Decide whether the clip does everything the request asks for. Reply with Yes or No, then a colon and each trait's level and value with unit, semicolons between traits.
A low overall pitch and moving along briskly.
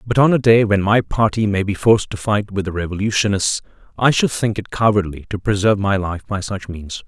Yes: low, 100 Hz; fast, 230 wpm